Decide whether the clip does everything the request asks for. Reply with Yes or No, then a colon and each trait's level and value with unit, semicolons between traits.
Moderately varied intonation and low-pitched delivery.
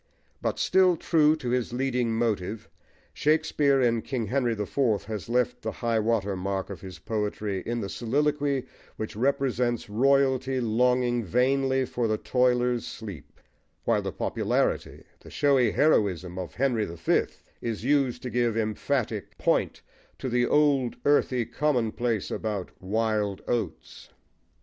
Yes: average, 3.7 semitones; low, 120 Hz